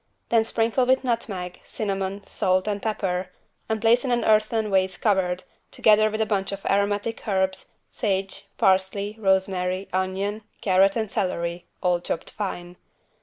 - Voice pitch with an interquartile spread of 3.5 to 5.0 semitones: No, narrow, 2.5 semitones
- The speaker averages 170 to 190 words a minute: No, average, 145 wpm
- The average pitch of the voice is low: No, high, 195 Hz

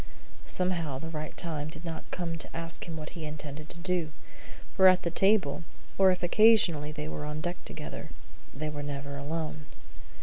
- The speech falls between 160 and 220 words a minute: Yes, average, 180 wpm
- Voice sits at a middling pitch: Yes, medium, 160 Hz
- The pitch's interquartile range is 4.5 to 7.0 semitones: No, average, 2.7 semitones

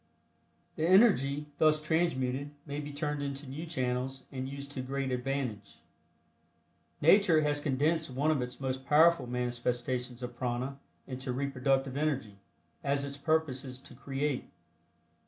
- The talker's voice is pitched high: No, medium, 140 Hz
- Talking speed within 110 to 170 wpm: Yes, slow, 135 wpm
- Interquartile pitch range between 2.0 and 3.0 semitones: Yes, narrow, 2.6 semitones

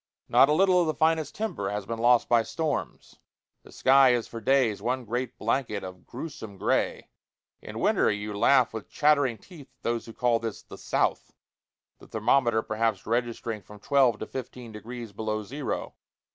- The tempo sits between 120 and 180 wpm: Yes, average, 175 wpm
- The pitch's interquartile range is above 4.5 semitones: No, average, 3.8 semitones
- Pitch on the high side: No, low, 120 Hz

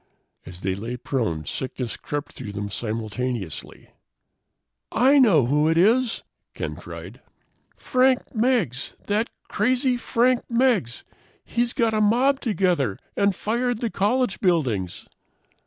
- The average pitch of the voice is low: No, high, 195 Hz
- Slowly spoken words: Yes, slow, 125 wpm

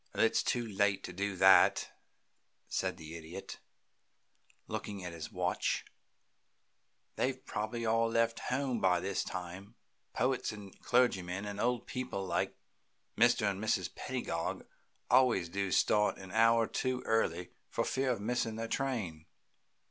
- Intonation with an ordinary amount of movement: Yes, average, 3.9 semitones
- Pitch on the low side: Yes, low, 105 Hz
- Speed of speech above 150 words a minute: No, average, 140 wpm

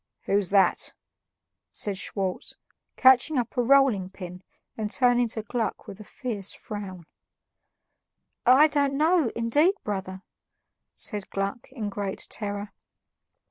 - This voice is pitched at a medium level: No, high, 215 Hz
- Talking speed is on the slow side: Yes, slow, 120 wpm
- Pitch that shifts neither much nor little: Yes, average, 4.6 semitones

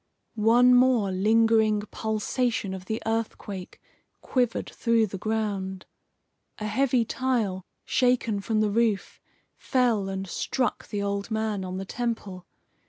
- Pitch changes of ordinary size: Yes, average, 3.0 semitones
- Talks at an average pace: No, slow, 125 wpm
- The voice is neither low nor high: No, high, 220 Hz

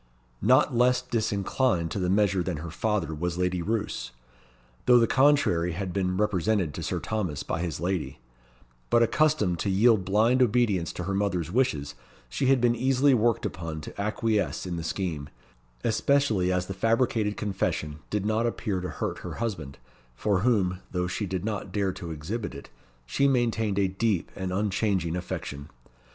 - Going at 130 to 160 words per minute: No, average, 170 wpm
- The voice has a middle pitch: No, low, 100 Hz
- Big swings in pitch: No, average, 4.4 semitones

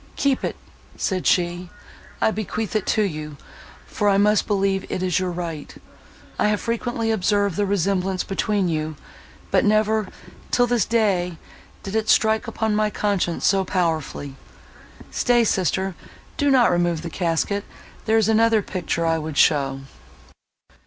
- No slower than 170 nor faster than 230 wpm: No, average, 145 wpm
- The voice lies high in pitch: Yes, high, 195 Hz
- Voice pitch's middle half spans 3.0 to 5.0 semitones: Yes, average, 3.8 semitones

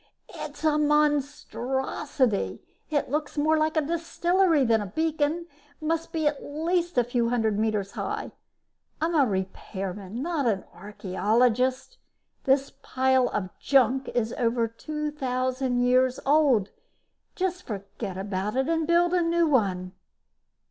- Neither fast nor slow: No, slow, 130 wpm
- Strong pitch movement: Yes, wide, 5.7 semitones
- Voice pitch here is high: Yes, very high, 265 Hz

